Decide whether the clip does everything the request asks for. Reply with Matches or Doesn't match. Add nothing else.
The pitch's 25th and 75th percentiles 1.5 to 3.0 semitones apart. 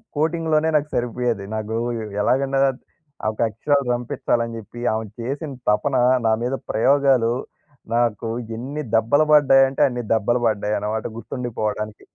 Doesn't match